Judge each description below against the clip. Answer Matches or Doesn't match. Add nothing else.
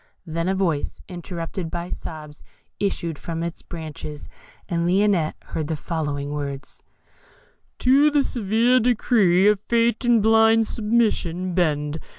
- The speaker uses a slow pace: Matches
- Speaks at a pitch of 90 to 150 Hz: Doesn't match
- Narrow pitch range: Doesn't match